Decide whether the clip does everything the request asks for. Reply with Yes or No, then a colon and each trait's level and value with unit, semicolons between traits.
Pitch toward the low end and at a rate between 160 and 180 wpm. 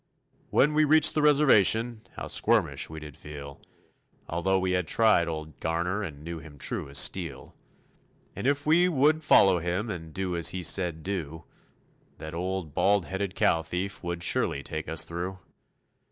Yes: very low, 90 Hz; average, 170 wpm